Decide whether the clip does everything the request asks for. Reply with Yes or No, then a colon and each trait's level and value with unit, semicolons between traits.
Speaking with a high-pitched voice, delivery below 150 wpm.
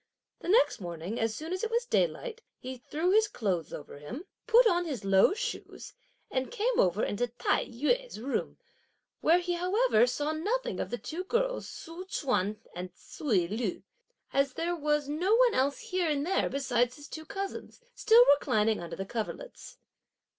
No: very high, 300 Hz; average, 175 wpm